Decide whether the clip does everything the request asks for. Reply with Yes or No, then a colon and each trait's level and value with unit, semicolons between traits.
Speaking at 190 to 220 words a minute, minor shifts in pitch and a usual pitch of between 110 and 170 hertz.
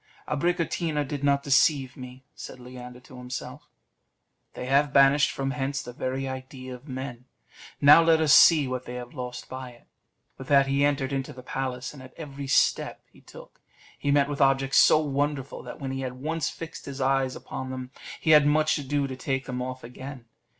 Yes: average, 195 wpm; narrow, 1.9 semitones; low, 135 Hz